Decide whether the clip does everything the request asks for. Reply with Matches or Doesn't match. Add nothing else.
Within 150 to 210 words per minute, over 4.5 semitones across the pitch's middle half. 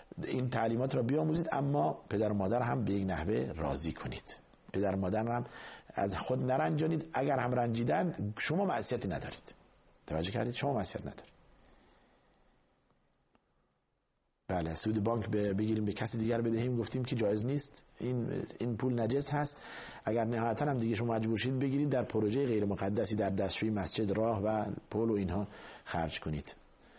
Doesn't match